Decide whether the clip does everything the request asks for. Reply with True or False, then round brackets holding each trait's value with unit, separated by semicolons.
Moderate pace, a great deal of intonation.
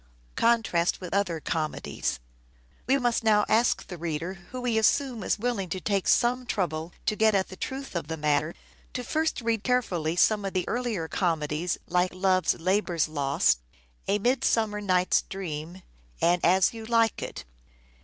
True (170 wpm; 5.7 semitones)